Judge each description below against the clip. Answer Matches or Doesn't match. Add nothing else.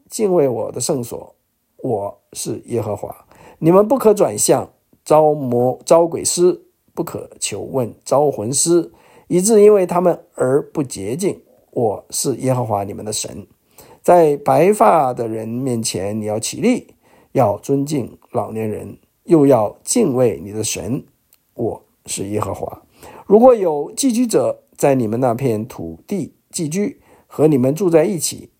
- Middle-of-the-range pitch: Matches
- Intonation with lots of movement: Matches